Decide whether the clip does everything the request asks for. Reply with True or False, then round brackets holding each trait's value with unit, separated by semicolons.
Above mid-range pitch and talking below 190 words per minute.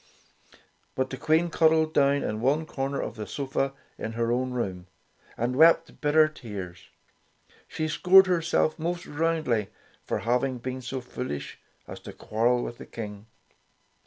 False (130 Hz; 150 wpm)